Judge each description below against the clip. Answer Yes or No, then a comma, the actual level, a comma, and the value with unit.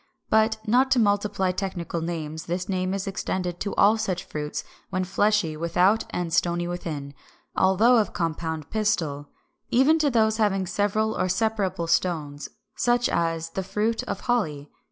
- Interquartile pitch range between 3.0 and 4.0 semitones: No, average, 4.4 semitones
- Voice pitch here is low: No, high, 190 Hz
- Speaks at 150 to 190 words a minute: Yes, average, 155 wpm